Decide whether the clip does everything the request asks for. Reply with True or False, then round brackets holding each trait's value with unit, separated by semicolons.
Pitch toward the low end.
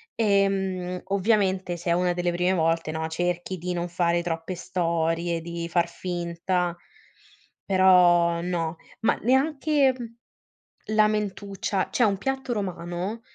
False (180 Hz)